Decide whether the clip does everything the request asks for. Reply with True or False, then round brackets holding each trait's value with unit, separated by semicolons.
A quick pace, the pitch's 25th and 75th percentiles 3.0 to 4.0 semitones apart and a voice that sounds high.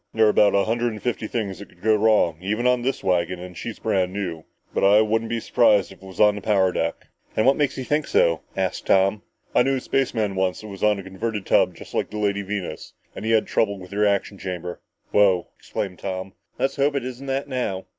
False (240 wpm; 3.4 semitones; 105 Hz)